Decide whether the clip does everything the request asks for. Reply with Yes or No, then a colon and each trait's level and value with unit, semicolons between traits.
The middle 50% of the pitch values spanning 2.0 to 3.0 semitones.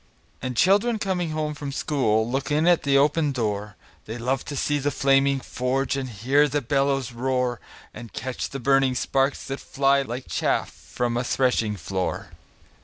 Yes: narrow, 2.6 semitones